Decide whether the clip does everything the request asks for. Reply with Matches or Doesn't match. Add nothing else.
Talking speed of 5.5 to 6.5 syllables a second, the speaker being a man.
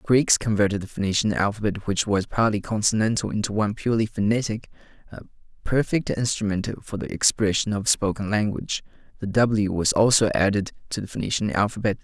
Matches